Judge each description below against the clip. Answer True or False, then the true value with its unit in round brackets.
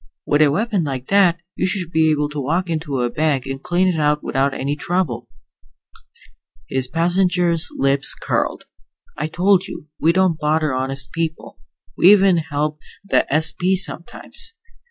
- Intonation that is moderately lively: True (3.9 semitones)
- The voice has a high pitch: False (160 Hz)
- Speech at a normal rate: True (155 wpm)